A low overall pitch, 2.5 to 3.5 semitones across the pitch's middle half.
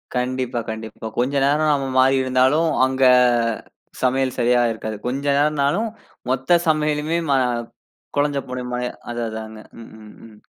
Yes: low, 130 Hz; average, 2.9 semitones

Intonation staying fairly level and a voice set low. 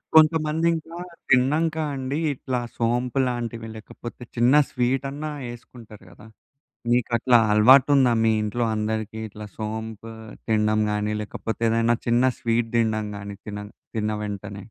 No: average, 3.1 semitones; low, 115 Hz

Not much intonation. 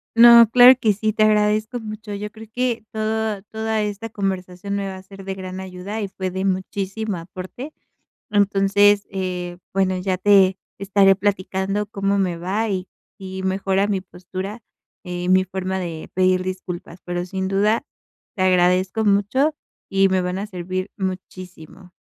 Yes: narrow, 2.0 semitones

